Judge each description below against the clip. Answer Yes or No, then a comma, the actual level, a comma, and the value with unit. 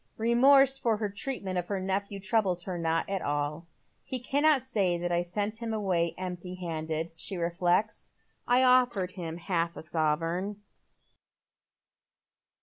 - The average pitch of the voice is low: No, medium, 185 Hz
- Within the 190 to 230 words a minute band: No, average, 145 wpm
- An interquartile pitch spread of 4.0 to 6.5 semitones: Yes, average, 4.5 semitones